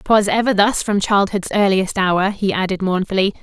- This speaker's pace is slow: No, average, 175 wpm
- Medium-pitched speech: No, high, 195 Hz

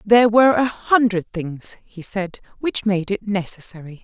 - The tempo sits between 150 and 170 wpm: Yes, average, 165 wpm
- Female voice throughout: Yes, female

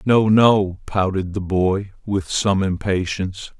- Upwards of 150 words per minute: No, slow, 135 wpm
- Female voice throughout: No, male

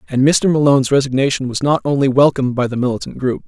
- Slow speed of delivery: No, fast, 205 wpm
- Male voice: Yes, male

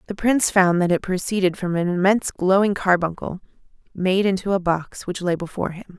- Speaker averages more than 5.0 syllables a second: Yes, 5.8 syllables/s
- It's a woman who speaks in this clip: Yes, female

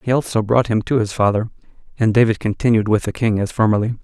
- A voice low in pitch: Yes, low, 110 Hz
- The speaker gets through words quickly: Yes, fast, 225 wpm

